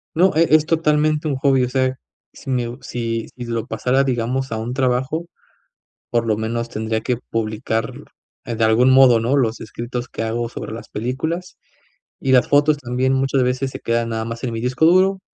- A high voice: No, low, 125 Hz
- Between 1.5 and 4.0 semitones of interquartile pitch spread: Yes, average, 2.8 semitones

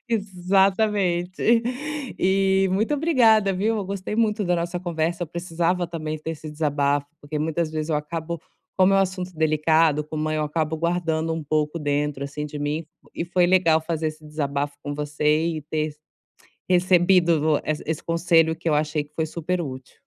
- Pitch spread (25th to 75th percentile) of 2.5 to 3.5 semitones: Yes, average, 3.1 semitones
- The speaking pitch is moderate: Yes, medium, 165 Hz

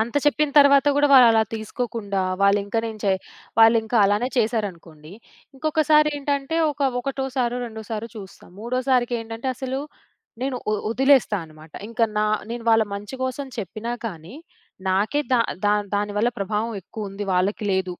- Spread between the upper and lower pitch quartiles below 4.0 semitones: No, average, 4.3 semitones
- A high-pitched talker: Yes, high, 225 Hz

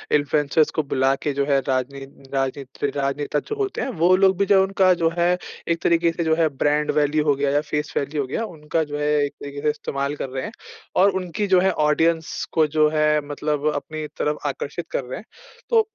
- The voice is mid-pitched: Yes, medium, 150 Hz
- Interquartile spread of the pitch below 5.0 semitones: Yes, average, 3.1 semitones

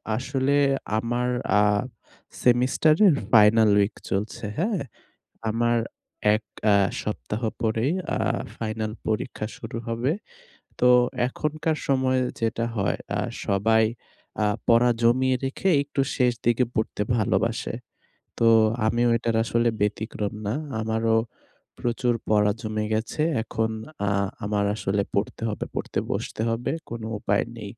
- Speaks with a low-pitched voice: Yes, low, 115 Hz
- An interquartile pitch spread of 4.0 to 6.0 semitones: No, narrow, 2.5 semitones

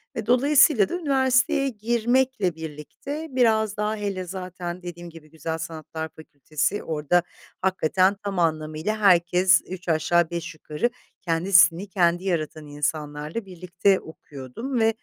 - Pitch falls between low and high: Yes, medium, 180 Hz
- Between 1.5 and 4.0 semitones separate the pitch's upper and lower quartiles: No, average, 5.1 semitones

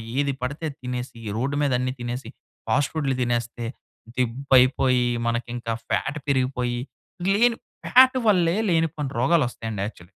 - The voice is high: No, low, 130 Hz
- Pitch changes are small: No, average, 3.2 semitones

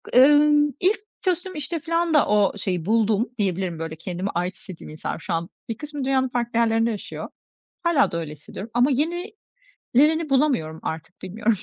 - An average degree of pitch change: No, wide, 8.3 semitones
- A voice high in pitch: Yes, high, 230 Hz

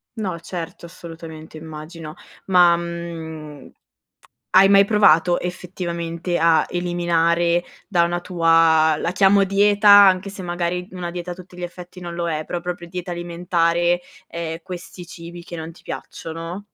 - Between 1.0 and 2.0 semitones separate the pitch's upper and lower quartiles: Yes, narrow, 1.4 semitones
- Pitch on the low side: No, medium, 175 Hz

